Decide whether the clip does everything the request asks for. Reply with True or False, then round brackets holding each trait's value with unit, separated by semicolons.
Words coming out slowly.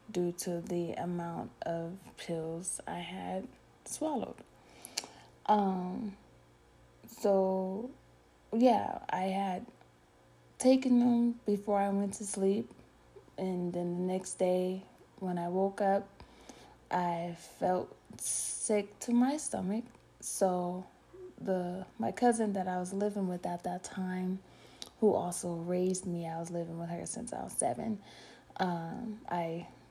True (125 wpm)